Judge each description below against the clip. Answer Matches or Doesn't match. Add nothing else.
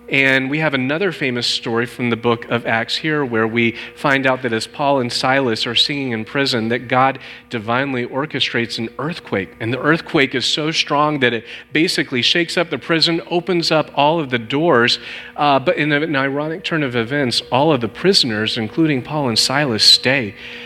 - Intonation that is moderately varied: Matches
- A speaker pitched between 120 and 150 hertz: Matches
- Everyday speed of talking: Matches